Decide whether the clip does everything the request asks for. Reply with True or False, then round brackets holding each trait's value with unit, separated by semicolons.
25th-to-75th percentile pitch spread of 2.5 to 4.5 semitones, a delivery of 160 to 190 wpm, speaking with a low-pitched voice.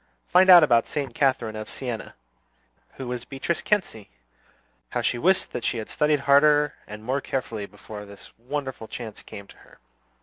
False (4.9 semitones; 170 wpm; 125 Hz)